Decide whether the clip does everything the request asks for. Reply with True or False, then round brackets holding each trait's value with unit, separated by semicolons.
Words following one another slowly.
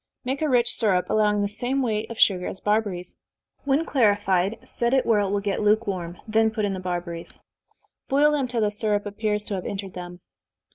False (200 wpm)